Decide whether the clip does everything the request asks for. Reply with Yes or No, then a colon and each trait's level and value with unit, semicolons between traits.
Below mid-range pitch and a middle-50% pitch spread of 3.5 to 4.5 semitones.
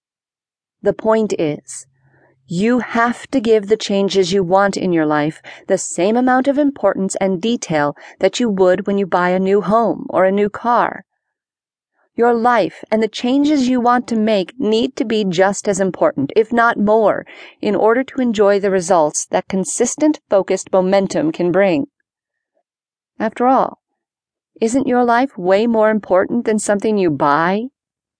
No: high, 210 Hz; average, 4.0 semitones